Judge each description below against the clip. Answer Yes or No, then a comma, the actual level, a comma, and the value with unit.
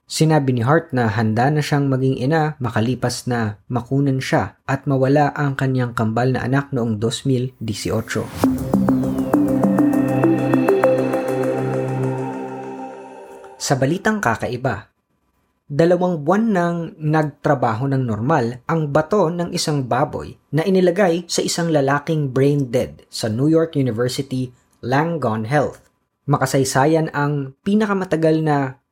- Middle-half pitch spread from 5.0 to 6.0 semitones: Yes, average, 5.3 semitones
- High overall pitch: No, low, 135 Hz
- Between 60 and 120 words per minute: Yes, slow, 110 wpm